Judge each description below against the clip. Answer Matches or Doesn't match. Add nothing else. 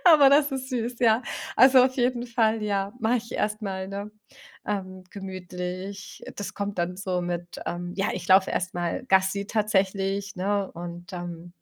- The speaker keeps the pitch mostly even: Doesn't match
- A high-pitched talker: Matches